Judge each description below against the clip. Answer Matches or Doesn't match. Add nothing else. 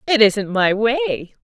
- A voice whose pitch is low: Doesn't match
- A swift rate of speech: Doesn't match